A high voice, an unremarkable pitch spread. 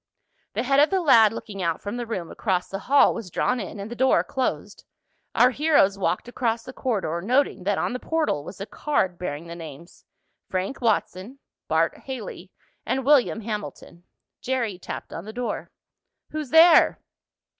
No: high, 225 Hz; wide, 6.0 semitones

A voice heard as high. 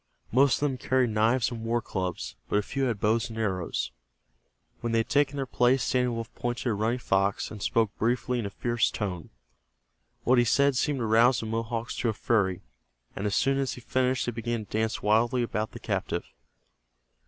No: low, 115 Hz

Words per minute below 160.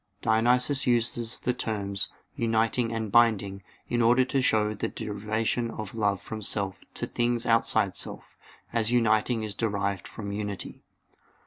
Yes: average, 140 wpm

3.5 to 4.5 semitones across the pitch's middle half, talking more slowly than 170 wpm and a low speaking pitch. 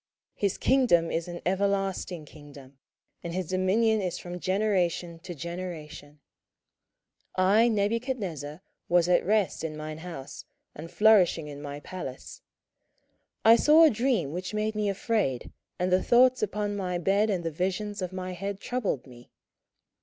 No: average, 4.1 semitones; average, 155 wpm; medium, 185 Hz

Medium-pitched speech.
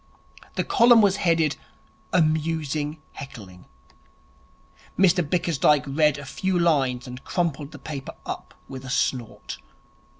Yes: medium, 150 Hz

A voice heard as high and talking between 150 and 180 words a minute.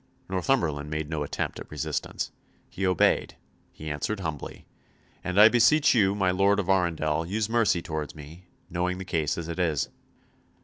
No: very low, 90 Hz; average, 165 wpm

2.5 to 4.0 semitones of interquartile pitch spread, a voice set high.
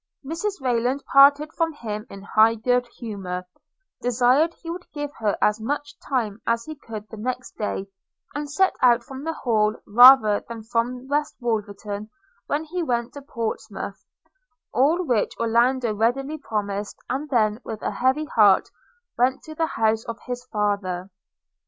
No: average, 4.7 semitones; high, 245 Hz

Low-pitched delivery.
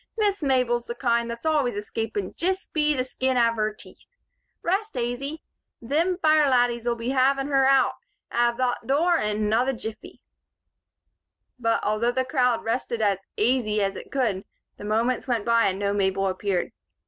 No: high, 240 Hz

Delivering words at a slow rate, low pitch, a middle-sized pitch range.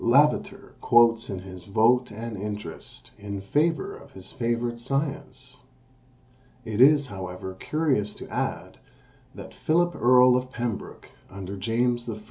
Yes: slow, 125 wpm; low, 120 Hz; average, 4.0 semitones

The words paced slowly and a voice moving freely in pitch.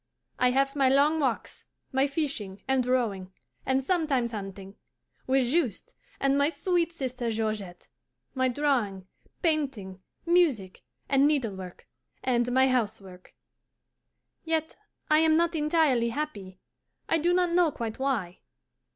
Yes: slow, 125 wpm; wide, 5.9 semitones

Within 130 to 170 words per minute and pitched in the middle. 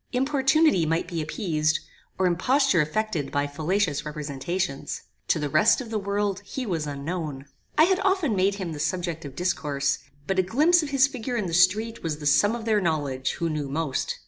No: average, 195 wpm; medium, 180 Hz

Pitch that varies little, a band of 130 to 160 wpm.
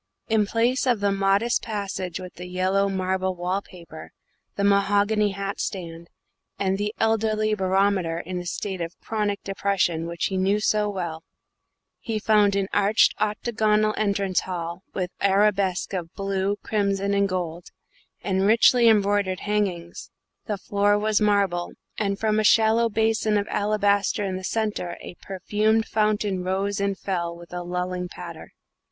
Yes: narrow, 2.3 semitones; average, 150 wpm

